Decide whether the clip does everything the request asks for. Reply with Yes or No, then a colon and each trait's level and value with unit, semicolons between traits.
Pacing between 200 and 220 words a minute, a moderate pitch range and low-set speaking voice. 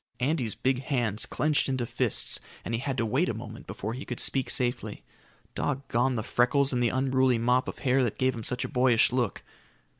No: fast, 205 wpm; narrow, 2.0 semitones; low, 125 Hz